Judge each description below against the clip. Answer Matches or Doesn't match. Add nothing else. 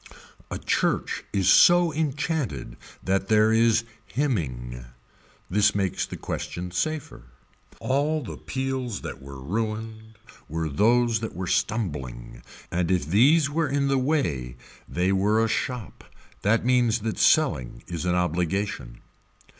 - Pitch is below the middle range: Matches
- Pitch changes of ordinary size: Doesn't match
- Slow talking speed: Matches